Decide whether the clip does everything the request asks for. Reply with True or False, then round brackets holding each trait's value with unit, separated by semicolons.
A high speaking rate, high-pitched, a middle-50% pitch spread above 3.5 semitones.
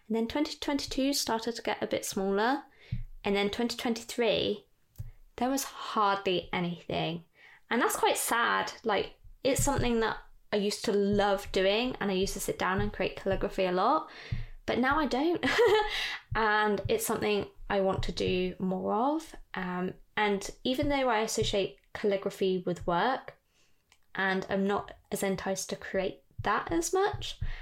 False (155 wpm; 205 Hz; 4.1 semitones)